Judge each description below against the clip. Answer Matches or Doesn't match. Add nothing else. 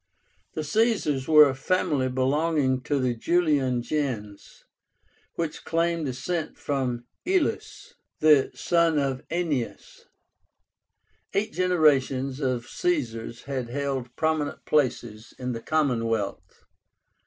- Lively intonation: Doesn't match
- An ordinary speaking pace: Doesn't match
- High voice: Doesn't match